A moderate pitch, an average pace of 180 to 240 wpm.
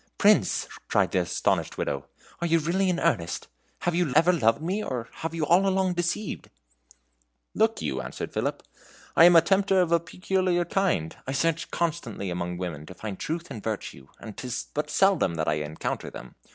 Yes: medium, 165 Hz; average, 185 wpm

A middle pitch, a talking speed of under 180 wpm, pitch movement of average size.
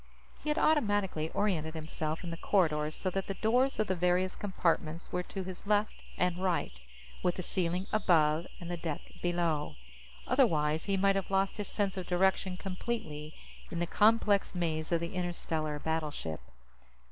Yes: medium, 180 Hz; average, 170 wpm; average, 3.5 semitones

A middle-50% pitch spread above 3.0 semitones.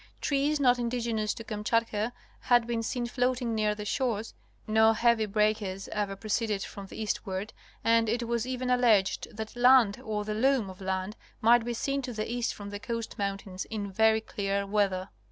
No: average, 2.7 semitones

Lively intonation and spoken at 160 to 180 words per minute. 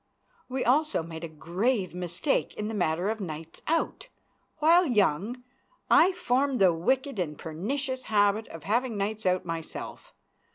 No: wide, 7.3 semitones; average, 150 wpm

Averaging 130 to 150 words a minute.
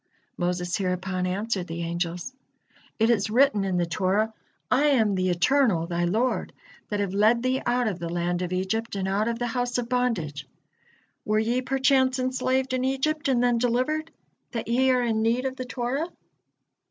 No: average, 180 wpm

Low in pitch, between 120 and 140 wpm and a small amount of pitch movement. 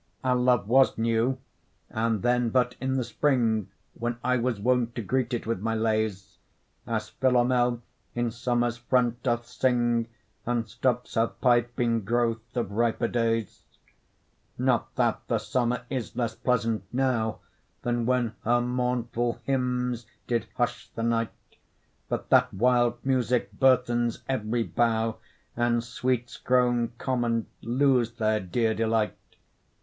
Yes: low, 120 Hz; slow, 135 wpm; narrow, 1.5 semitones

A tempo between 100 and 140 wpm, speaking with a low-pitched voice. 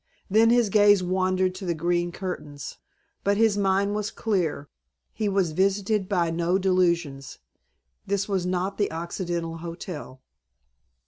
No: slow, 135 wpm; medium, 185 Hz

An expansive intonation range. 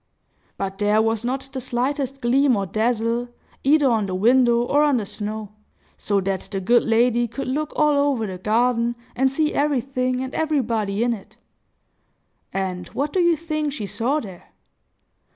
No: average, 4.2 semitones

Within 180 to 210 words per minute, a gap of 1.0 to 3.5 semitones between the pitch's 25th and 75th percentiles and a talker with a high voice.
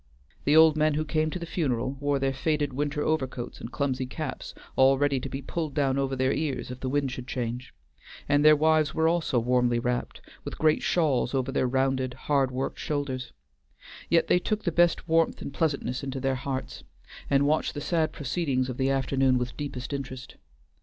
No: average, 195 wpm; average, 2.9 semitones; low, 135 Hz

